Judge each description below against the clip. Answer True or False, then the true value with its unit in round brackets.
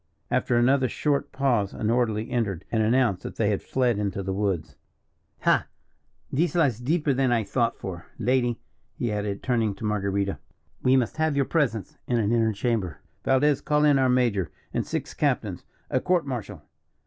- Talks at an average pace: True (175 wpm)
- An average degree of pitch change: True (4.3 semitones)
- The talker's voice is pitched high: False (120 Hz)